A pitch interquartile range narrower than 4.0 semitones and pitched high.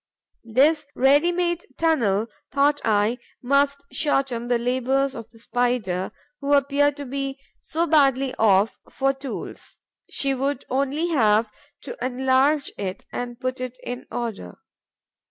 Yes: average, 2.8 semitones; very high, 265 Hz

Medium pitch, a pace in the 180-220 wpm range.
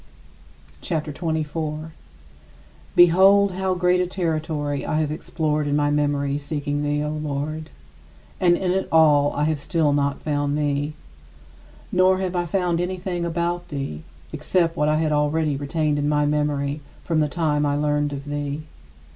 No: medium, 150 Hz; average, 160 wpm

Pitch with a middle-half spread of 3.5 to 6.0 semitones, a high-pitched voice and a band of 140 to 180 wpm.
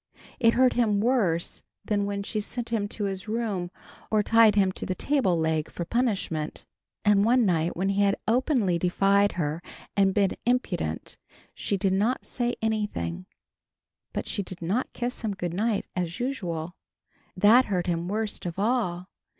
Yes: average, 4.3 semitones; high, 200 Hz; average, 165 wpm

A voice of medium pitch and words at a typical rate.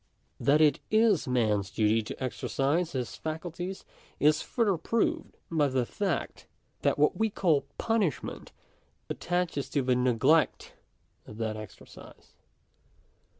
No: medium, 150 Hz; slow, 120 wpm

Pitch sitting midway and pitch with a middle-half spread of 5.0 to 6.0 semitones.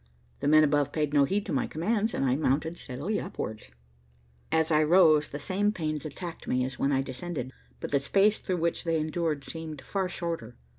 No: medium, 155 Hz; average, 3.7 semitones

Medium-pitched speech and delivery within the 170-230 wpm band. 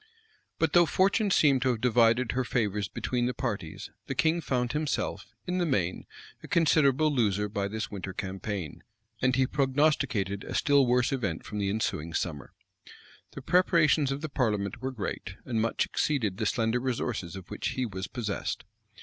No: low, 125 Hz; average, 175 wpm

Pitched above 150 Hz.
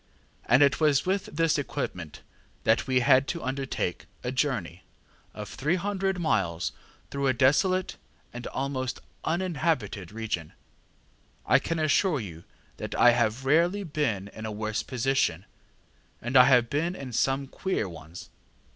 No: low, 135 Hz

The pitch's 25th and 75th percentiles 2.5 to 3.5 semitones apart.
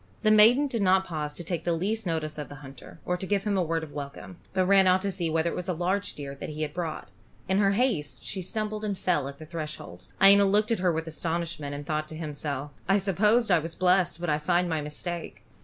No: average, 4.1 semitones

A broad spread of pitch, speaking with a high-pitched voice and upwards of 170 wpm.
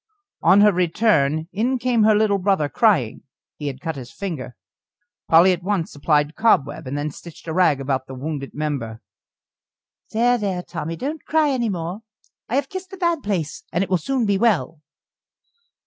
No: wide, 6.8 semitones; medium, 180 Hz; average, 180 wpm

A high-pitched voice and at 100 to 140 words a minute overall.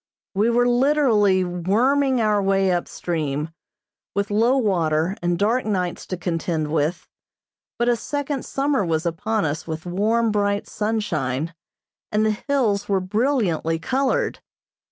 Yes: high, 200 Hz; slow, 135 wpm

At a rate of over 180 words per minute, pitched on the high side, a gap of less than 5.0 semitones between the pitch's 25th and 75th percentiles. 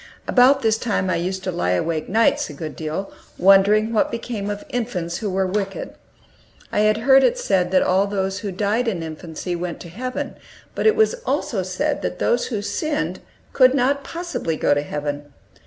No: average, 190 wpm; high, 200 Hz; wide, 5.6 semitones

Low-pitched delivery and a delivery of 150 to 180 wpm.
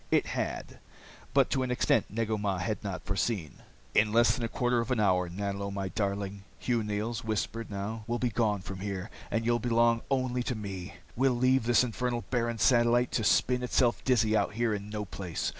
No: low, 110 Hz; average, 200 wpm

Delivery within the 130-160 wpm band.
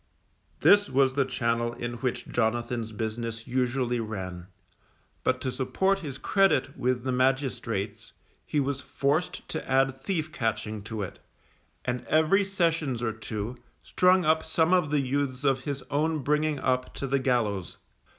Yes: average, 150 wpm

